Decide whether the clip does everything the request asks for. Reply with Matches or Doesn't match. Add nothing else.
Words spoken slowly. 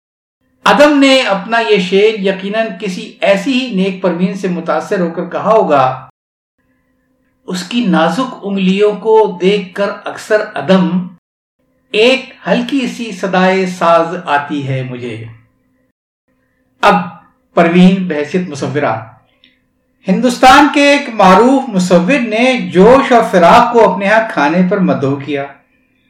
Doesn't match